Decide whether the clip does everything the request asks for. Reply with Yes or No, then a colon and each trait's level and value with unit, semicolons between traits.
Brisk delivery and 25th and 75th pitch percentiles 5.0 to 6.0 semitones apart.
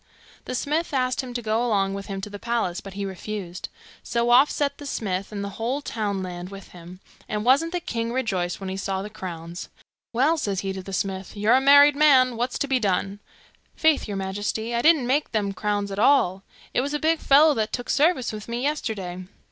Yes: fast, 220 wpm; average, 5.3 semitones